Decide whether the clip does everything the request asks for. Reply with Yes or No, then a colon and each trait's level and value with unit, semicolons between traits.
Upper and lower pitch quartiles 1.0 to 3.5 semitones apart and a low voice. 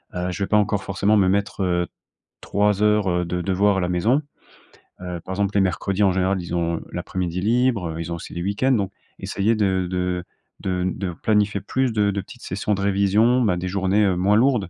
Yes: narrow, 2.4 semitones; very low, 95 Hz